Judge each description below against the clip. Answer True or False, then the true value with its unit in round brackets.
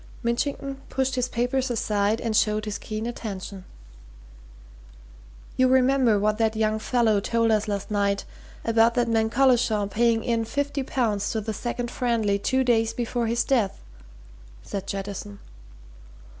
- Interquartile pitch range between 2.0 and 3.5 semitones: True (2.6 semitones)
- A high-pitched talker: True (225 Hz)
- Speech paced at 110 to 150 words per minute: True (145 wpm)